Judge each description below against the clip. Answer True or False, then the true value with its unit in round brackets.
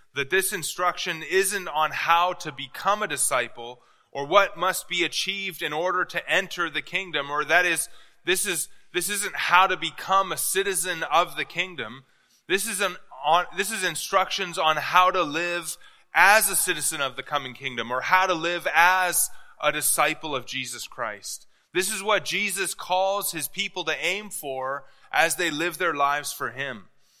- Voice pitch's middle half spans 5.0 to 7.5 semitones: False (4.1 semitones)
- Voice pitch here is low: False (180 Hz)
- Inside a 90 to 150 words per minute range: False (180 wpm)